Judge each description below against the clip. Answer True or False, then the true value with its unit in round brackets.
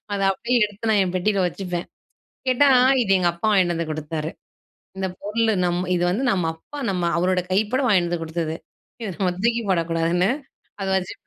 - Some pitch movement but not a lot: True (3.4 semitones)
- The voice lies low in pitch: False (185 Hz)